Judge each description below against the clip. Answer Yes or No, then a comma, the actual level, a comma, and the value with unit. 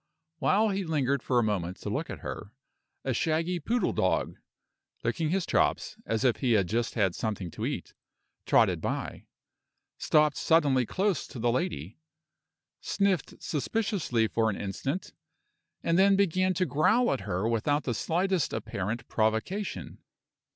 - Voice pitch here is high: No, medium, 140 Hz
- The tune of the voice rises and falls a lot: Yes, wide, 8.6 semitones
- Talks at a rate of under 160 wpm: Yes, average, 150 wpm